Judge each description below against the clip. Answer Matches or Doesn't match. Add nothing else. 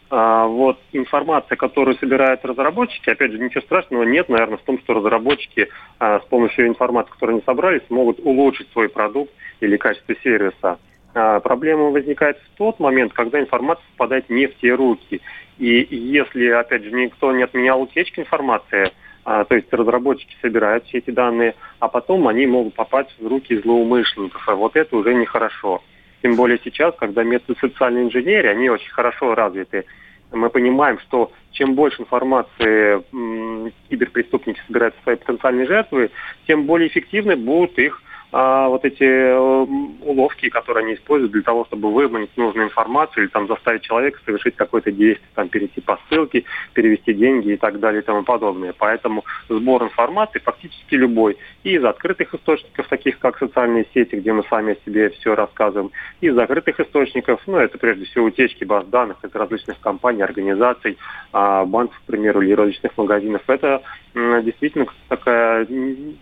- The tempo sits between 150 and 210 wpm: Matches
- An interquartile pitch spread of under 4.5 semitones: Matches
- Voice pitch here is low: Matches